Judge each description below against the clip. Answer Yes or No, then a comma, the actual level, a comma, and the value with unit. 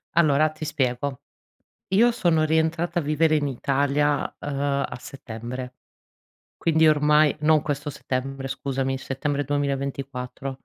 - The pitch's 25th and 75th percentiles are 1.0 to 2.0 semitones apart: No, narrow, 2.4 semitones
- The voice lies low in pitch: No, medium, 145 Hz